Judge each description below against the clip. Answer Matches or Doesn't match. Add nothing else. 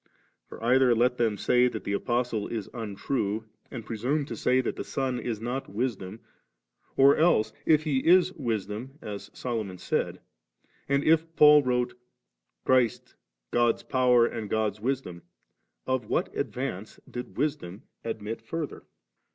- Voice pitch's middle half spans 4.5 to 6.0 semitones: Doesn't match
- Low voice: Matches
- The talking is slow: Doesn't match